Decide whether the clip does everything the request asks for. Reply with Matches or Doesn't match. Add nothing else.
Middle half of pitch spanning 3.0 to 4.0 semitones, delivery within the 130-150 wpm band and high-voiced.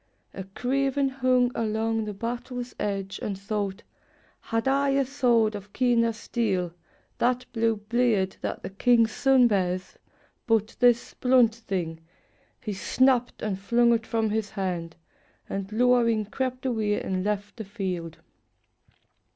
Matches